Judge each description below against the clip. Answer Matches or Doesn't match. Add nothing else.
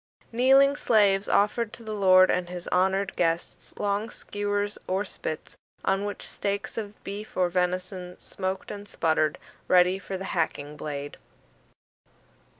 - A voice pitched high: Matches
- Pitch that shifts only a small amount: Matches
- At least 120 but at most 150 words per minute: Matches